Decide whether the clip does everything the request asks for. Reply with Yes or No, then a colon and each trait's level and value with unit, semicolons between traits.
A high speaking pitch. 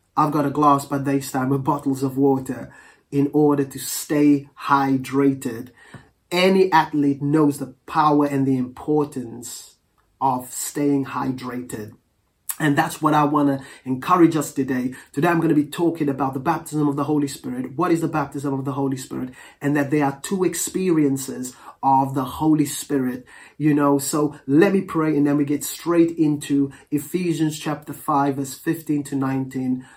No: medium, 145 Hz